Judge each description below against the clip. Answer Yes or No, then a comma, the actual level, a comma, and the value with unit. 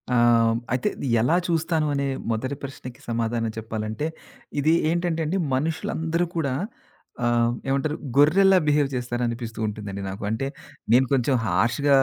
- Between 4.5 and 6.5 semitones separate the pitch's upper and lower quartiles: Yes, average, 4.9 semitones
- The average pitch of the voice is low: Yes, low, 130 Hz